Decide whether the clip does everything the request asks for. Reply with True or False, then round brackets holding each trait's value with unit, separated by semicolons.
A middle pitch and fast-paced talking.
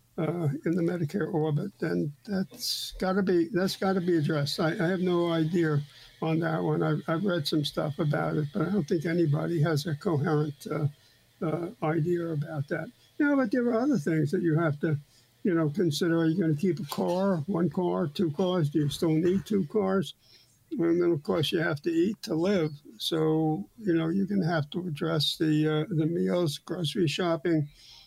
True (165 Hz; 210 wpm)